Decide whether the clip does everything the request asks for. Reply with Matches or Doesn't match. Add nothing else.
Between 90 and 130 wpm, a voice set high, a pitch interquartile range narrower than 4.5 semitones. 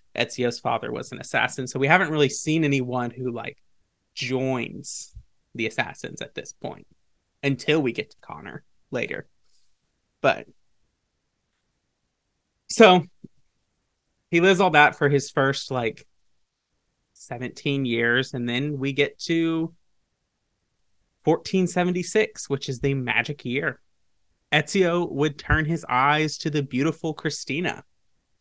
Doesn't match